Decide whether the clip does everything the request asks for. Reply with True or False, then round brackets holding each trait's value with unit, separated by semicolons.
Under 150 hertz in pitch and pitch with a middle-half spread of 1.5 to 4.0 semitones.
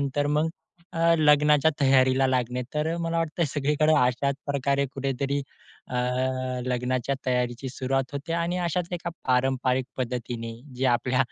True (135 Hz; 2.8 semitones)